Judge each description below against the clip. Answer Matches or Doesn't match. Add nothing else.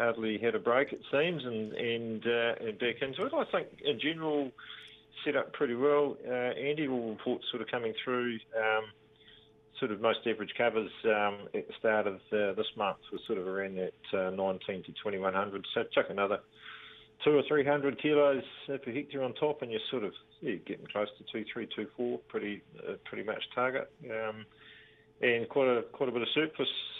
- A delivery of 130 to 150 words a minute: Doesn't match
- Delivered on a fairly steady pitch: Doesn't match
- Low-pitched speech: Matches